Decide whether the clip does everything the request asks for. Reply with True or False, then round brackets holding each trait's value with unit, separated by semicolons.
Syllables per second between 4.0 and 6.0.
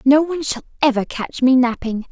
True (5.4 syllables/s)